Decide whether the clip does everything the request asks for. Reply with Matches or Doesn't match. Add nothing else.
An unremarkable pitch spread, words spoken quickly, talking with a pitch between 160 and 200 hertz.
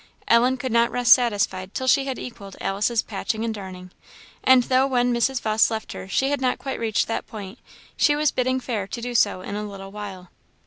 Doesn't match